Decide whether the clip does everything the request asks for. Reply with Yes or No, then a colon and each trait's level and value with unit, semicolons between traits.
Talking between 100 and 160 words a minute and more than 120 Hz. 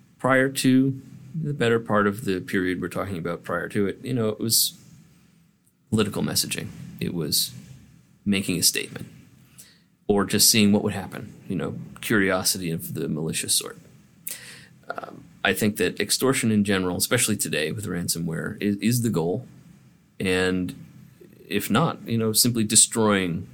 No: average, 155 wpm; low, 110 Hz